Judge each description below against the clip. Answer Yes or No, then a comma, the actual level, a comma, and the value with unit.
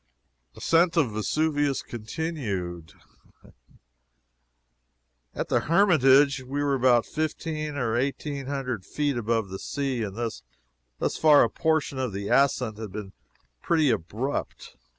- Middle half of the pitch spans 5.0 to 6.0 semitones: Yes, wide, 5.4 semitones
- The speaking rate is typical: No, slow, 120 wpm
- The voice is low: Yes, low, 130 Hz